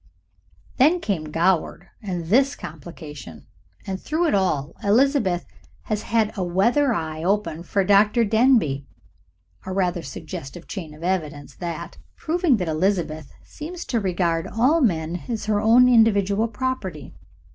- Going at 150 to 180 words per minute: No, slow, 135 wpm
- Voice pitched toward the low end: No, high, 190 Hz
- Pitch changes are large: Yes, wide, 5.8 semitones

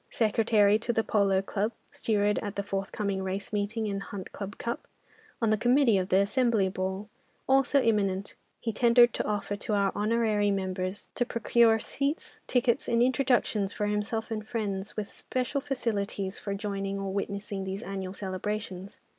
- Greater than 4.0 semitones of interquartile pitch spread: No, average, 2.7 semitones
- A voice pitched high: Yes, high, 210 Hz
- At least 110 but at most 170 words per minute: Yes, average, 165 wpm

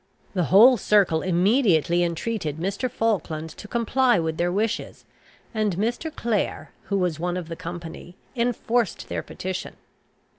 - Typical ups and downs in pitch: Yes, average, 4.9 semitones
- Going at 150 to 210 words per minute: No, average, 140 wpm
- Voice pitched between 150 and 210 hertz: Yes, high, 190 Hz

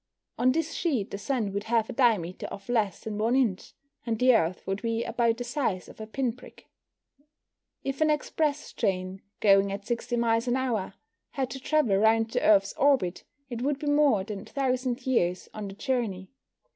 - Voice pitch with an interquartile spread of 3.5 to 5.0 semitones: Yes, average, 4.6 semitones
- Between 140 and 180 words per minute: No, average, 190 wpm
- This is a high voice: Yes, high, 230 Hz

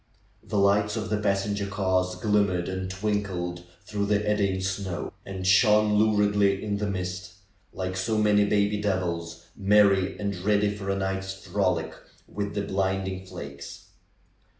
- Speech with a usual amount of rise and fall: No, narrow, 1.7 semitones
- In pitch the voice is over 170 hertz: No, low, 100 Hz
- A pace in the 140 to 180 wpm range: Yes, average, 145 wpm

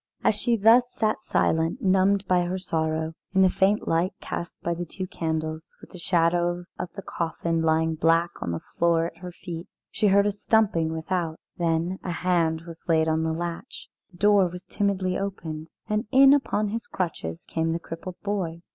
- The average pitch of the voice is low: No, medium, 175 Hz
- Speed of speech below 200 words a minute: Yes, average, 190 wpm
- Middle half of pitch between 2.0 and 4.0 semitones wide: Yes, average, 3.1 semitones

